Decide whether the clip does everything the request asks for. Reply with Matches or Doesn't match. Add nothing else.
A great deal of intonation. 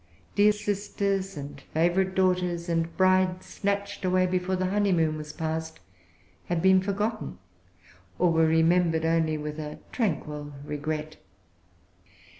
Doesn't match